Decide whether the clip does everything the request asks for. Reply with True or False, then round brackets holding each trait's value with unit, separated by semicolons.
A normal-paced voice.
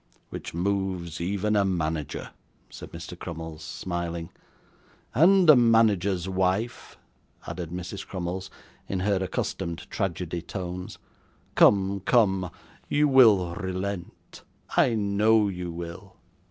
False (110 wpm)